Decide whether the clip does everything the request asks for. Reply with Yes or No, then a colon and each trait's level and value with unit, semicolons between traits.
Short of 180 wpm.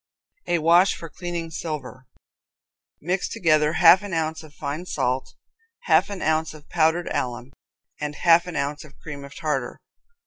Yes: average, 160 wpm